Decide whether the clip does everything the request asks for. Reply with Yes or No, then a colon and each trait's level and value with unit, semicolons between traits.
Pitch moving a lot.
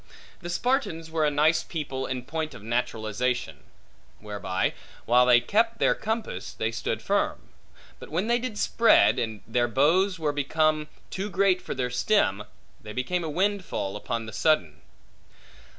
Yes: wide, 7.5 semitones